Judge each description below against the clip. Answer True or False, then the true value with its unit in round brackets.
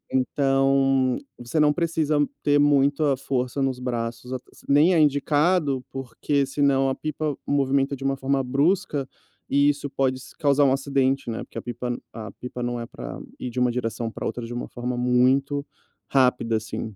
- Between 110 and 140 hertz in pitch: True (135 Hz)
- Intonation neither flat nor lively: False (2.3 semitones)